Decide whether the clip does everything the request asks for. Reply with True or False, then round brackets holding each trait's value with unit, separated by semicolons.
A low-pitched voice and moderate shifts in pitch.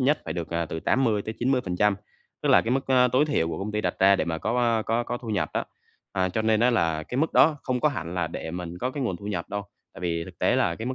False (105 Hz; 6.1 semitones)